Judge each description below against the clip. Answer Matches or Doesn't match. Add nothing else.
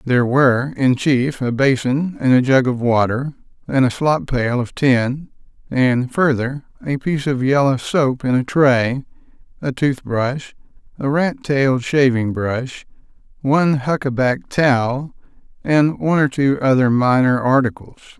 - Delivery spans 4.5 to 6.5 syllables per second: Doesn't match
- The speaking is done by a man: Matches